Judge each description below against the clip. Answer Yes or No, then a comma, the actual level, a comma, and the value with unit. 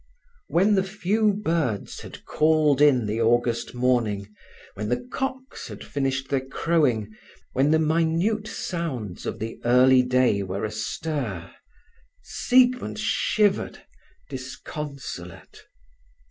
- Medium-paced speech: No, slow, 110 wpm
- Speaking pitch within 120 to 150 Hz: Yes, low, 135 Hz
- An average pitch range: No, wide, 6.5 semitones